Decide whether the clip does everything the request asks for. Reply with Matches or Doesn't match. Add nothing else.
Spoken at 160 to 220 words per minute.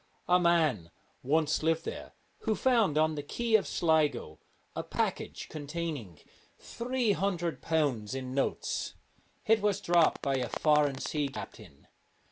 Doesn't match